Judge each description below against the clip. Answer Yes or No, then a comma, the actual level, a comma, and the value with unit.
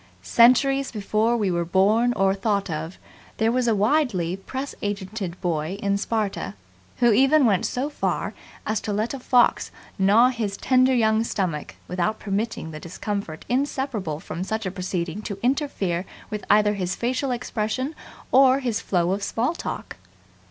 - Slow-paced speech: No, average, 160 wpm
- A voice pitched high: Yes, high, 215 Hz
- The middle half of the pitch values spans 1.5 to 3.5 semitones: No, average, 4.5 semitones